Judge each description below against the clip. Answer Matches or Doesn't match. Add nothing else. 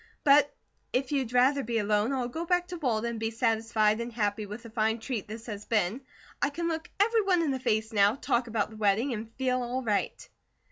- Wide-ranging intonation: Doesn't match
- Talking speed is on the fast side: Matches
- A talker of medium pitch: Doesn't match